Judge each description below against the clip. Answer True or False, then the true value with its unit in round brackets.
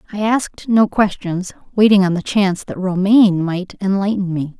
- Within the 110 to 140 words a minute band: False (155 wpm)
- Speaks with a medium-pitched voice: False (195 Hz)